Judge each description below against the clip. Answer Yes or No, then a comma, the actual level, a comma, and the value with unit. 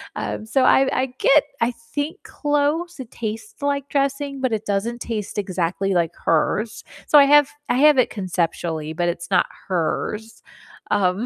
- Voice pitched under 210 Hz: No, high, 225 Hz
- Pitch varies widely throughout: Yes, wide, 7.0 semitones